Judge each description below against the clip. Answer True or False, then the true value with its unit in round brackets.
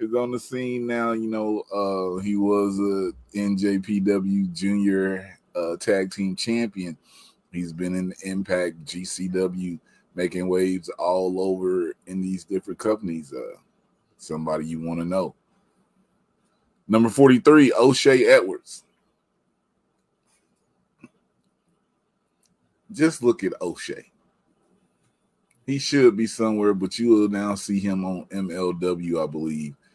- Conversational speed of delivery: False (115 wpm)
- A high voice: False (100 Hz)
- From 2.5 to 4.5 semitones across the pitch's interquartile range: True (4.1 semitones)